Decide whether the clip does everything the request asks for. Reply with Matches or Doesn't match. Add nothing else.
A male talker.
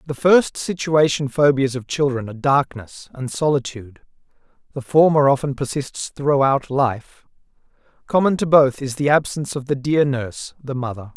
Matches